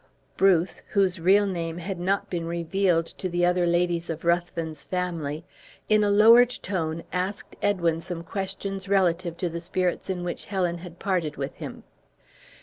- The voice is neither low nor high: Yes, medium, 175 Hz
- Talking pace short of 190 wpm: Yes, average, 160 wpm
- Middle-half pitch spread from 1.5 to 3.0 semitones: Yes, narrow, 2.4 semitones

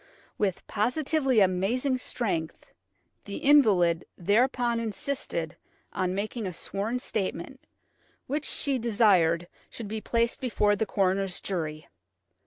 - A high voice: Yes, high, 210 Hz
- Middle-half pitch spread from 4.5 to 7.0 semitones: Yes, average, 5.0 semitones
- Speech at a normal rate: No, slow, 110 wpm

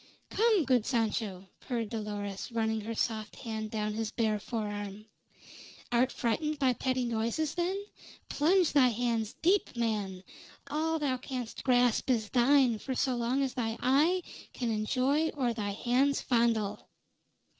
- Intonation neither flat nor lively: Yes, average, 3.6 semitones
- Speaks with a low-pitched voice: No, high, 240 Hz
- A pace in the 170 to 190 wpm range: No, average, 145 wpm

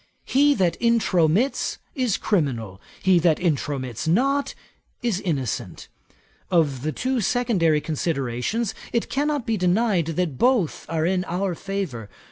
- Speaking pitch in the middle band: Yes, medium, 180 Hz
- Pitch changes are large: Yes, wide, 7.3 semitones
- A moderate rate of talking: No, slow, 125 wpm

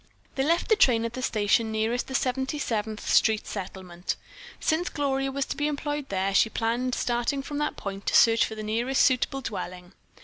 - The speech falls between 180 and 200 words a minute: Yes, average, 195 wpm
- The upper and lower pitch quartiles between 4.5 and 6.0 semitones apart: No, average, 4.1 semitones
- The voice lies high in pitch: Yes, high, 240 Hz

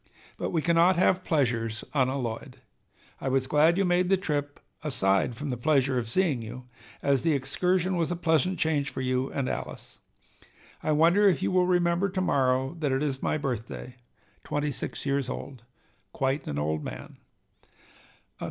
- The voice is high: No, medium, 145 Hz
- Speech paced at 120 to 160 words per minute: No, average, 170 wpm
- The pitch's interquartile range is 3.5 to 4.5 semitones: No, average, 5.0 semitones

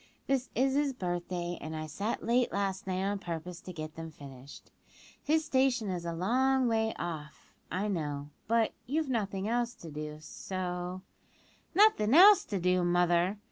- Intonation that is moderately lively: No, wide, 5.9 semitones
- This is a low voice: No, high, 190 Hz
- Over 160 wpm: Yes, average, 170 wpm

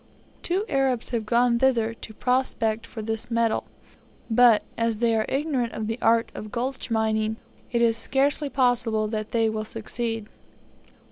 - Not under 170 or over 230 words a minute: No, average, 155 wpm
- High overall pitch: Yes, high, 230 Hz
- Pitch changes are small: Yes, narrow, 2.1 semitones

